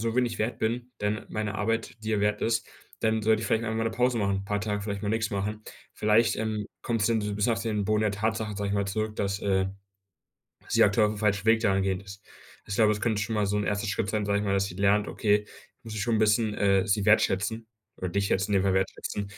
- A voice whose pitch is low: Yes, low, 105 Hz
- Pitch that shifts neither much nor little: No, narrow, 1.7 semitones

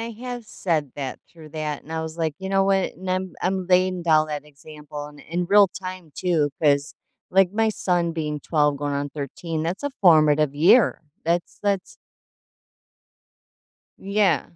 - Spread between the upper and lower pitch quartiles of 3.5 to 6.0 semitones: Yes, average, 3.9 semitones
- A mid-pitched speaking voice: Yes, medium, 165 Hz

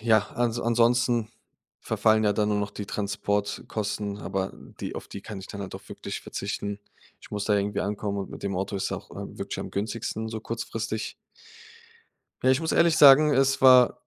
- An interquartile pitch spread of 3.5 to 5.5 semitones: No, average, 2.7 semitones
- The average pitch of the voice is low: Yes, low, 105 Hz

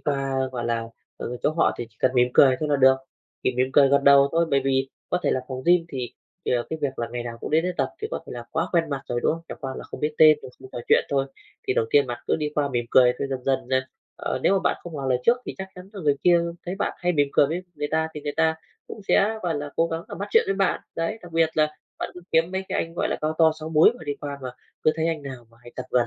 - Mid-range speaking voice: Yes, medium, 145 Hz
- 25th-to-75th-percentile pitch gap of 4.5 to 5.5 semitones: No, average, 4.0 semitones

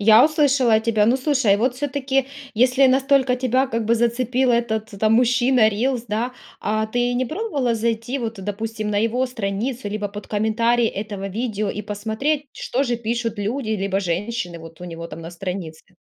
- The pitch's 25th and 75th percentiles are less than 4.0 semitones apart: Yes, average, 3.5 semitones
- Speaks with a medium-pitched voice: No, high, 230 Hz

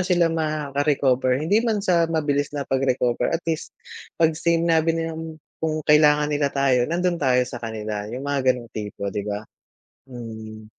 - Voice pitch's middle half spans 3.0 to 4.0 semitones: No, average, 4.6 semitones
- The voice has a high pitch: No, medium, 145 Hz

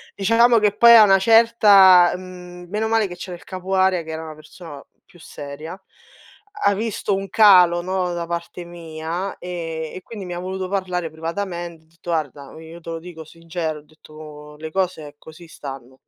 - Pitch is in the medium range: Yes, medium, 175 Hz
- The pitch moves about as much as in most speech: Yes, average, 3.0 semitones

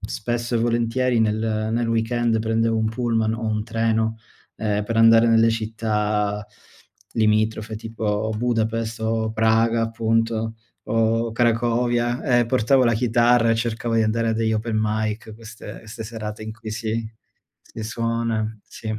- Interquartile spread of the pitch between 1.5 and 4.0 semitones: No, narrow, 1.0 semitones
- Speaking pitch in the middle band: No, low, 115 Hz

